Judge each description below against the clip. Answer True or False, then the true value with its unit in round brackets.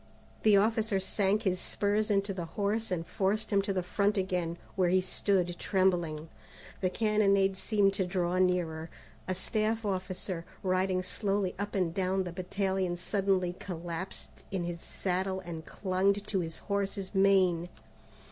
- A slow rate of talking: False (150 wpm)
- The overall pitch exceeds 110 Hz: True (190 Hz)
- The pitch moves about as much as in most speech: False (1.9 semitones)